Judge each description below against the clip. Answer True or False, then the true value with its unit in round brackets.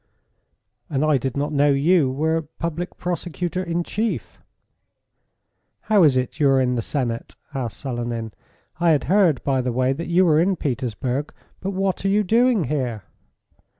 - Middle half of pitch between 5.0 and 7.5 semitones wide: True (5.4 semitones)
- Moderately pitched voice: True (150 Hz)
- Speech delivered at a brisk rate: False (165 wpm)